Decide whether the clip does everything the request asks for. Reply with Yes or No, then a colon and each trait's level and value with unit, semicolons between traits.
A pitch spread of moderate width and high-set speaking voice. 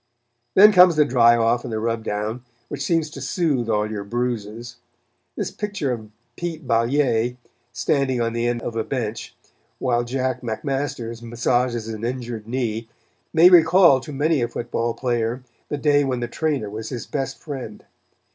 No: average, 3.5 semitones; low, 120 Hz